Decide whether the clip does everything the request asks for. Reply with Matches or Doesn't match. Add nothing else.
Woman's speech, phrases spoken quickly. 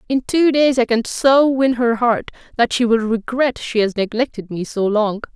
Matches